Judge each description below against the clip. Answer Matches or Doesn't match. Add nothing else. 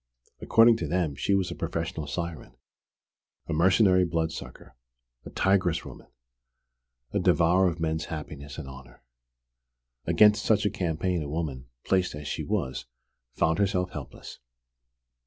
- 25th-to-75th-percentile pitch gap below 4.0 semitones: Matches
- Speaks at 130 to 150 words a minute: Matches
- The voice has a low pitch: Matches